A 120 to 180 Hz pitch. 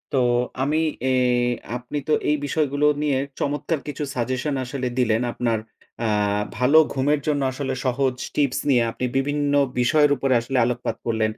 Yes: low, 135 Hz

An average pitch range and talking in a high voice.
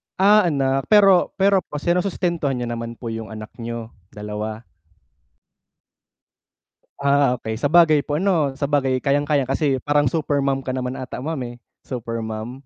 No: average, 4.4 semitones; low, 135 Hz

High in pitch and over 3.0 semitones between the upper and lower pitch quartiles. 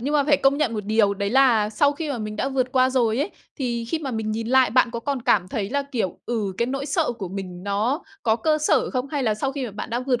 Yes: high, 245 Hz; average, 4.0 semitones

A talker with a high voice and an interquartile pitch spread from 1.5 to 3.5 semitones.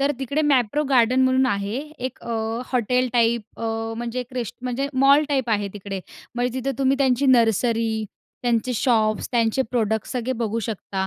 Yes: high, 245 Hz; narrow, 2.6 semitones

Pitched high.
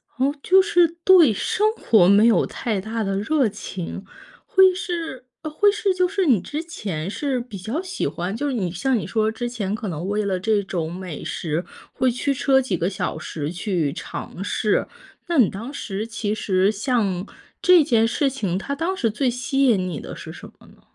Yes: high, 225 Hz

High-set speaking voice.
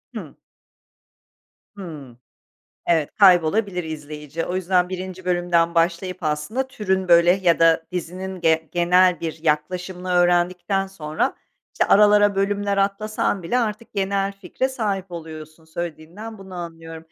No: medium, 180 Hz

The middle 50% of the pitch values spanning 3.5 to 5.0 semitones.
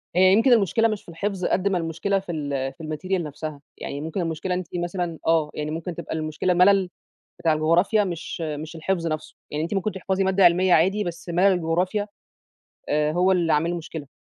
No: average, 3.1 semitones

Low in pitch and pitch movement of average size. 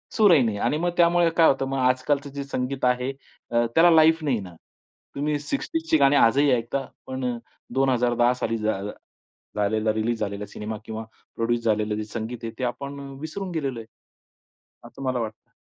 Yes: low, 125 Hz; average, 3.9 semitones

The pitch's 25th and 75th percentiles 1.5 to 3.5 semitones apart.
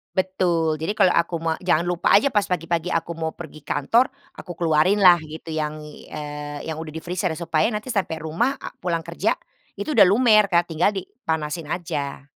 Yes: average, 2.9 semitones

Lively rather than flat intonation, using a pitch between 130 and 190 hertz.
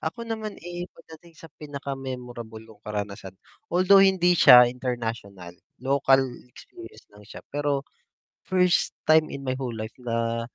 Yes: wide, 6.6 semitones; low, 135 Hz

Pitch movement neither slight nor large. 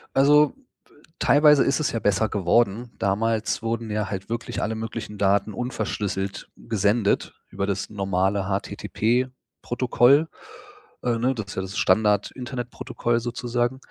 Yes: average, 3.3 semitones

